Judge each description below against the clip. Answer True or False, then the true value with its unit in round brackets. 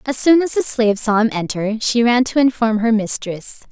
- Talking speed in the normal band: False (225 wpm)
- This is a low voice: False (230 Hz)